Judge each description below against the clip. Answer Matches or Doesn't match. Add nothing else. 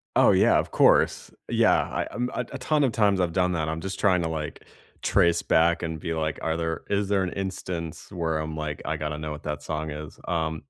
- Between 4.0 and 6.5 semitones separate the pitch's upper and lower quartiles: Doesn't match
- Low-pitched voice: Matches